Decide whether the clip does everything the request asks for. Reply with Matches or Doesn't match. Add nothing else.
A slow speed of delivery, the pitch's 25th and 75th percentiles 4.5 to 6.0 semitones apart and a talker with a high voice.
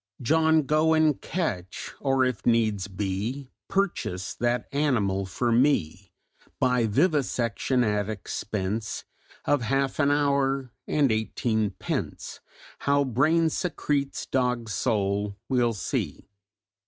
Doesn't match